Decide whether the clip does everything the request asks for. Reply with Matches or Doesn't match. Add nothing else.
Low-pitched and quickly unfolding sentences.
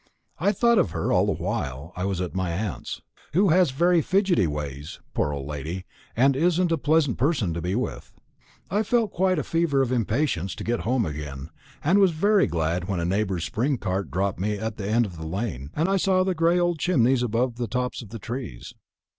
Matches